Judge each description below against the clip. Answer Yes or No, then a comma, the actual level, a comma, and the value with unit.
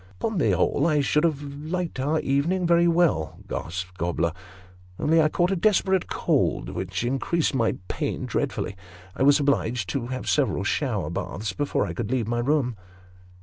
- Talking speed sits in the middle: Yes, average, 180 wpm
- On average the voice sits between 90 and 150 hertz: Yes, medium, 140 Hz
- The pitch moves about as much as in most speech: No, wide, 6.4 semitones